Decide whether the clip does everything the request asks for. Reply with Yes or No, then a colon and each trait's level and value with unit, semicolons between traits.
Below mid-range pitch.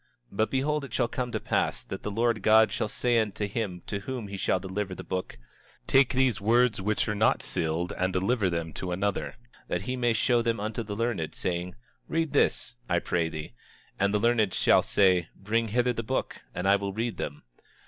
Yes: low, 105 Hz